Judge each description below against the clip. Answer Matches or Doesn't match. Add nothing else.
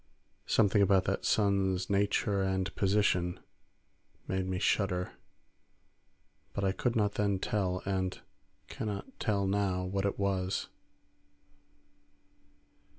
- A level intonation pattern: Matches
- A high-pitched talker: Doesn't match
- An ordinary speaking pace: Doesn't match